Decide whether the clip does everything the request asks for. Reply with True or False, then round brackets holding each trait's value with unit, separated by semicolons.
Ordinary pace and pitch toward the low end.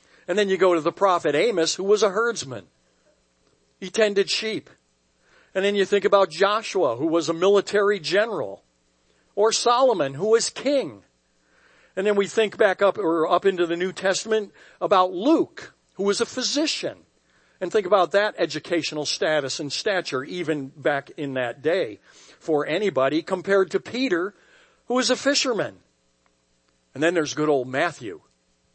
False (160 wpm; 185 Hz)